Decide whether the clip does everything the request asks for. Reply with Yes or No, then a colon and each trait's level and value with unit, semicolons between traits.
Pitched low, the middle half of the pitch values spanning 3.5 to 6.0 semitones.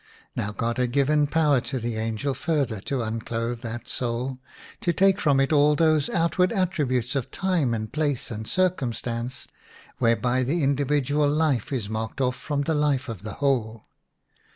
Yes: low, 130 Hz; average, 4.1 semitones